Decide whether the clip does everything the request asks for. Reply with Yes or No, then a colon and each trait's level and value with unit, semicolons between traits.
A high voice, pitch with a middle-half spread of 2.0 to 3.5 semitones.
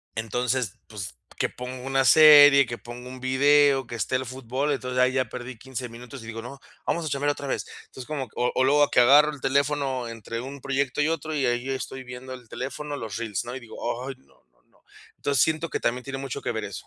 No: low, 130 Hz; narrow, 2.5 semitones